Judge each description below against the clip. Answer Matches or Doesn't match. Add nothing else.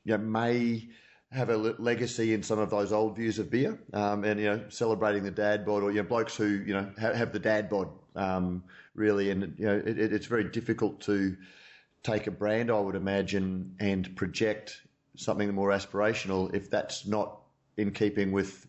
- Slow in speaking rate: Doesn't match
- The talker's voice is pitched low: Matches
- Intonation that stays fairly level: Matches